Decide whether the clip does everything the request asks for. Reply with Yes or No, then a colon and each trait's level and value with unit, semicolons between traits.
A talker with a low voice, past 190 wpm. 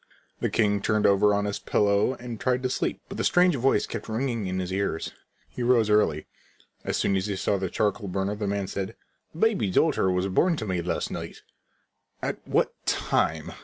Yes: low, 105 Hz; average, 200 wpm